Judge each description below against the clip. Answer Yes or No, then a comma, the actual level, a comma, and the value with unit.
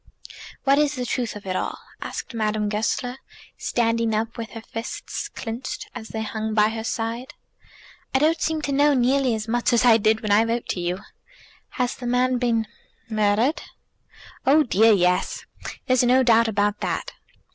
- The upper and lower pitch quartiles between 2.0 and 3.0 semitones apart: Yes, narrow, 2.6 semitones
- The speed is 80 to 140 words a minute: No, average, 175 wpm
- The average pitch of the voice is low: No, high, 230 Hz